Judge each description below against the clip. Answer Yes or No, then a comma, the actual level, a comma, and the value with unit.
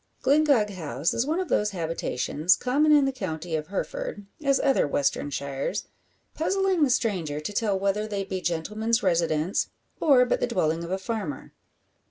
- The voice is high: Yes, high, 200 Hz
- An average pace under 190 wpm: Yes, average, 170 wpm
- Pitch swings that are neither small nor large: No, wide, 8.1 semitones